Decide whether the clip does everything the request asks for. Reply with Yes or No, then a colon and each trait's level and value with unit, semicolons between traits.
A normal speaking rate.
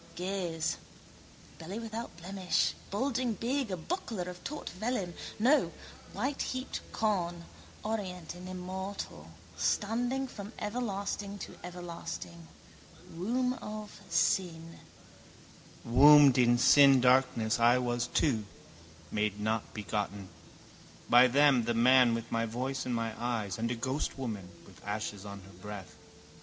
No: slow, 120 wpm